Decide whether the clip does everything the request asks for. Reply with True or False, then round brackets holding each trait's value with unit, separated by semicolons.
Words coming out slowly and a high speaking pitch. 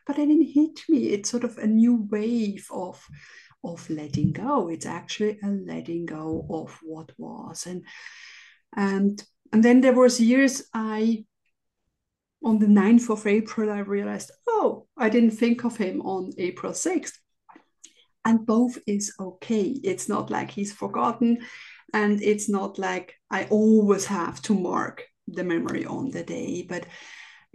False (155 wpm; 215 Hz)